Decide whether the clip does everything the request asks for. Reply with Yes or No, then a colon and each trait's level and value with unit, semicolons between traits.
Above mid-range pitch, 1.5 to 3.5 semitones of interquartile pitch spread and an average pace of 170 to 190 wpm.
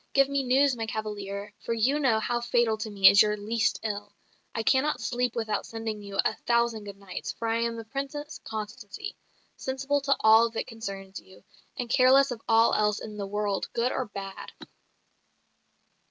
Yes: high, 225 Hz; average, 3.0 semitones; average, 185 wpm